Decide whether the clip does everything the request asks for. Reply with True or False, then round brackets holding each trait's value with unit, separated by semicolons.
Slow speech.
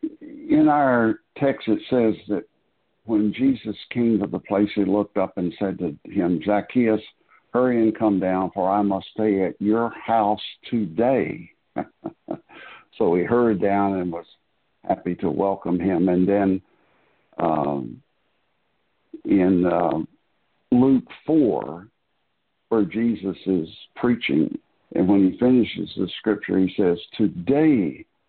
True (130 wpm)